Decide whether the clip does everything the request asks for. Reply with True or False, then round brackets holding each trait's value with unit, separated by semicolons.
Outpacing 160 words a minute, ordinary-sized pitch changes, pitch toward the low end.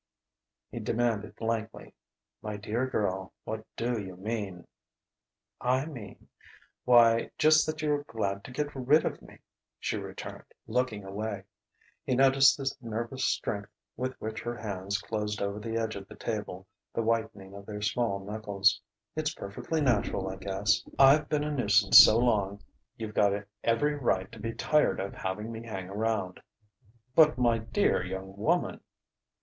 False (155 wpm; 3.9 semitones; 110 Hz)